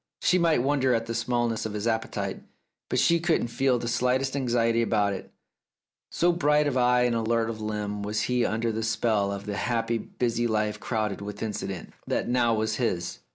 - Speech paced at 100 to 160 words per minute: No, average, 200 wpm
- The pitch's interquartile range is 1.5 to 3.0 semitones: Yes, narrow, 2.6 semitones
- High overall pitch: No, low, 115 Hz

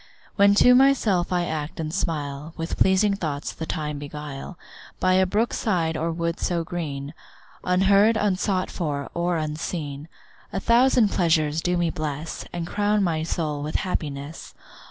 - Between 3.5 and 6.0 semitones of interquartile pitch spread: Yes, average, 3.9 semitones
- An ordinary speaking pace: Yes, average, 155 wpm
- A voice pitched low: No, medium, 170 Hz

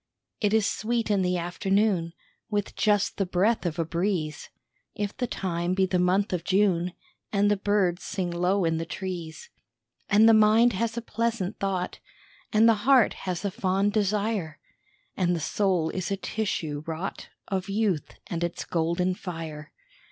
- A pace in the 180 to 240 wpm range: No, average, 165 wpm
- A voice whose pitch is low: No, high, 190 Hz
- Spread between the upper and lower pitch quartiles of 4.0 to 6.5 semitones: No, average, 3.2 semitones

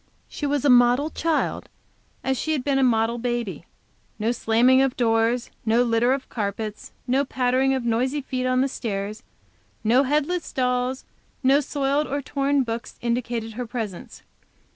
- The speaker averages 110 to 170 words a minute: Yes, average, 160 wpm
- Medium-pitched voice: No, very high, 250 Hz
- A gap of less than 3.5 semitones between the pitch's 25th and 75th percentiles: Yes, average, 2.8 semitones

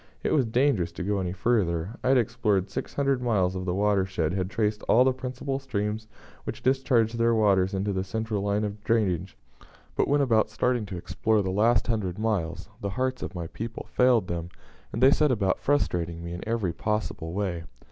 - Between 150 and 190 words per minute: No, average, 200 wpm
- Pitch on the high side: No, low, 105 Hz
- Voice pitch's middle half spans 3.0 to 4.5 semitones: Yes, average, 4.1 semitones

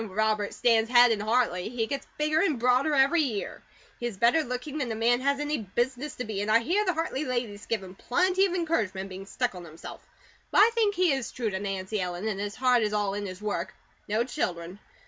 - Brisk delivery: Yes, fast, 235 wpm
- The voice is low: No, high, 235 Hz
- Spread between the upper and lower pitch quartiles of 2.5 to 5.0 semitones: No, wide, 5.4 semitones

